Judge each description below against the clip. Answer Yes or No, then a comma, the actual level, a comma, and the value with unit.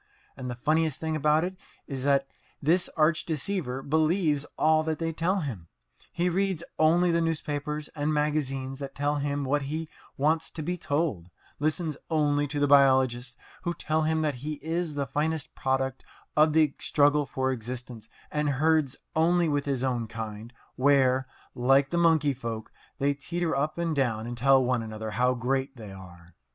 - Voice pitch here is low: No, medium, 145 Hz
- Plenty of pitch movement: No, average, 3.3 semitones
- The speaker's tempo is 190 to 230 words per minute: No, average, 175 wpm